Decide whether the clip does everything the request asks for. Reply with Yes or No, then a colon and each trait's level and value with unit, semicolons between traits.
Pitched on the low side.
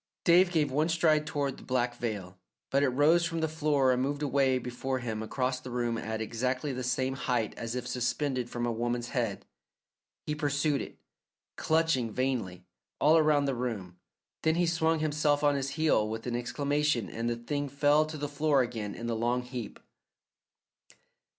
Yes: low, 130 Hz